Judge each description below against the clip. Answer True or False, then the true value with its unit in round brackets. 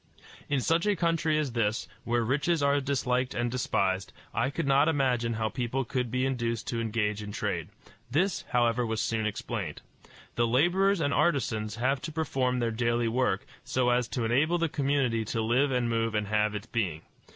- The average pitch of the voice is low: True (125 Hz)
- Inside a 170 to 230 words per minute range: True (185 wpm)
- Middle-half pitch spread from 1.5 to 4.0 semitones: True (3.7 semitones)